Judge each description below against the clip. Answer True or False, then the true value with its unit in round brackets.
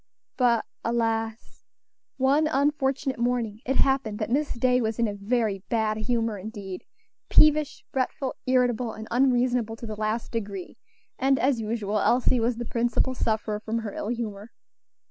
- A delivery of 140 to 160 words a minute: True (150 wpm)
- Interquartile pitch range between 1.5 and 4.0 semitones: True (2.7 semitones)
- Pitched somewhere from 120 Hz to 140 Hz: False (235 Hz)